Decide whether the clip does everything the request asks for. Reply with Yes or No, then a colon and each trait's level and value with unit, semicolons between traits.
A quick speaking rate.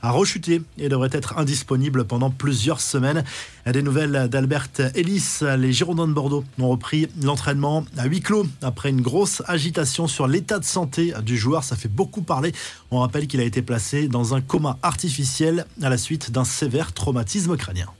No: average, 180 wpm